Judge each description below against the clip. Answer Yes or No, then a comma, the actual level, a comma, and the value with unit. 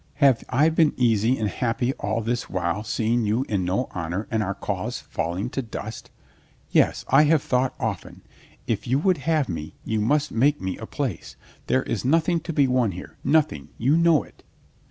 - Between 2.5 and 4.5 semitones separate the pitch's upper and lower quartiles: No, average, 5.3 semitones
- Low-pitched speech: Yes, low, 120 Hz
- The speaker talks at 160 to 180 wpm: No, average, 190 wpm